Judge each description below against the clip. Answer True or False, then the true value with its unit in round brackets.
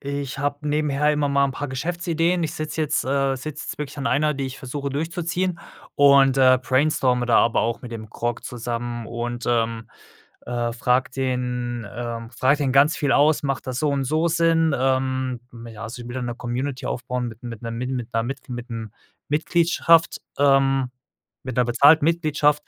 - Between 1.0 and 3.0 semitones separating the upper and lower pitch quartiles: False (3.5 semitones)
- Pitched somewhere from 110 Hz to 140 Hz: True (135 Hz)